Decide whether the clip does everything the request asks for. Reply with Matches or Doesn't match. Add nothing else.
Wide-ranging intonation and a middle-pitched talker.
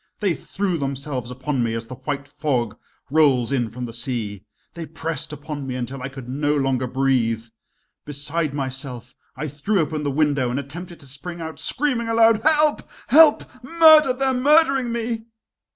Matches